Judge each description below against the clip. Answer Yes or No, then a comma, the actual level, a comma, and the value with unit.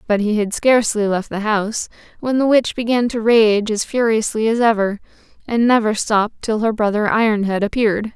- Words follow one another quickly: No, average, 185 wpm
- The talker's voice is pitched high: Yes, high, 220 Hz